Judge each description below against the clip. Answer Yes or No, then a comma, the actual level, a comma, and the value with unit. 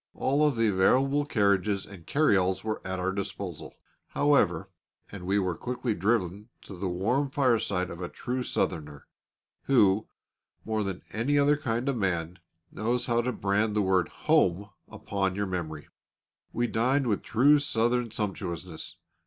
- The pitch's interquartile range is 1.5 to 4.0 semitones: No, average, 4.7 semitones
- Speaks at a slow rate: No, average, 155 wpm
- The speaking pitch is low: Yes, low, 105 Hz